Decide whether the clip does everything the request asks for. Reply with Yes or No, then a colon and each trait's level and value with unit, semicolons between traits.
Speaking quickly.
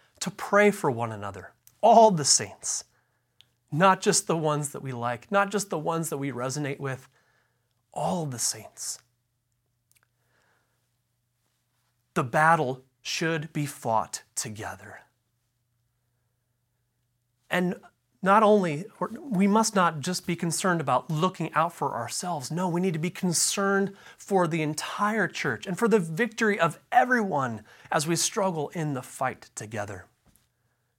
No: slow, 135 wpm